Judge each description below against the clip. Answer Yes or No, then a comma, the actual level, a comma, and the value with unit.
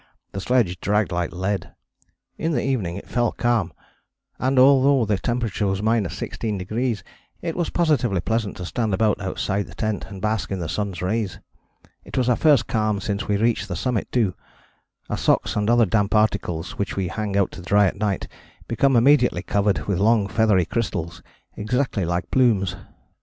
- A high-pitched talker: No, low, 105 Hz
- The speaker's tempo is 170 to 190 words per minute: Yes, average, 175 wpm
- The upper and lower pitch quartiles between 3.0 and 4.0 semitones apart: Yes, average, 3.6 semitones